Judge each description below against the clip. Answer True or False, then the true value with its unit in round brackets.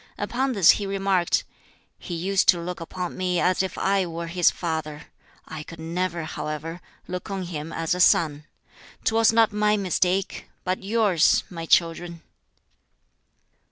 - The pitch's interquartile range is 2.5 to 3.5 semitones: True (2.9 semitones)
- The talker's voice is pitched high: False (180 Hz)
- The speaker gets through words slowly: False (150 wpm)